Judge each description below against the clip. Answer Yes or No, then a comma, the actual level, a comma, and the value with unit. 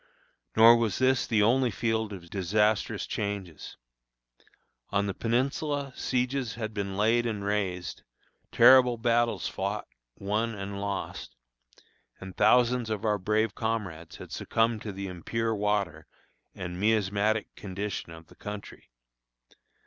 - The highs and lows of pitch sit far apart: No, average, 2.8 semitones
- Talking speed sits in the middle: No, slow, 125 wpm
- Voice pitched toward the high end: No, low, 105 Hz